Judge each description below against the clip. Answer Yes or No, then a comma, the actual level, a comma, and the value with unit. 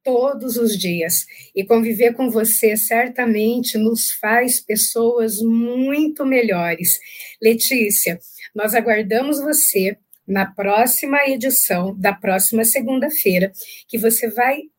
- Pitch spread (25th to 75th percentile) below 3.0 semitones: No, average, 3.3 semitones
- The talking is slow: Yes, slow, 105 wpm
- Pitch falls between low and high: No, high, 230 Hz